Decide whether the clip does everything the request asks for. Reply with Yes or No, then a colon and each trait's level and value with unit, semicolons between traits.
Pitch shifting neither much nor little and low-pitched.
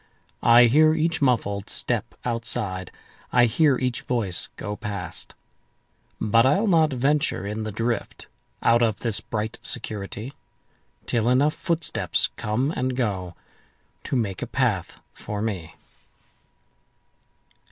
Yes: average, 4.0 semitones; low, 115 Hz